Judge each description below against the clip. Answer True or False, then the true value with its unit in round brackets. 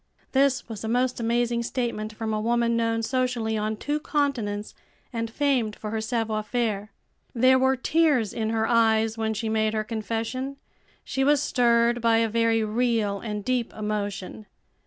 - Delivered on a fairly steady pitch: True (2.2 semitones)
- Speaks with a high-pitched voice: True (230 Hz)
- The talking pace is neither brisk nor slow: True (165 wpm)